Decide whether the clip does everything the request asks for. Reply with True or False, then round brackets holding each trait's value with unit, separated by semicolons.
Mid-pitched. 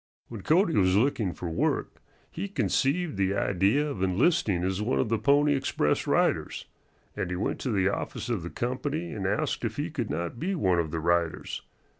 False (110 Hz)